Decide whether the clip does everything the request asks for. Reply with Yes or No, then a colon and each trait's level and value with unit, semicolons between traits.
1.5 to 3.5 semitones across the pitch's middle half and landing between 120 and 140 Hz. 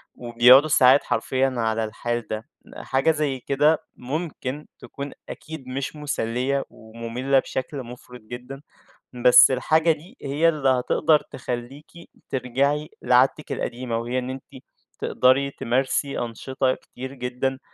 Yes: narrow, 2.4 semitones; low, 130 Hz